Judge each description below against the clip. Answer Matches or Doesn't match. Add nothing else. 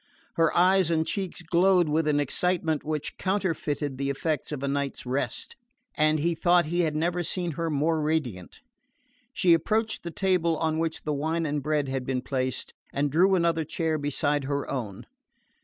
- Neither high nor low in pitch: Matches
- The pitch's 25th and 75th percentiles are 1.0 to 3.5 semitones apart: Matches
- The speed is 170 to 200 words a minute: Matches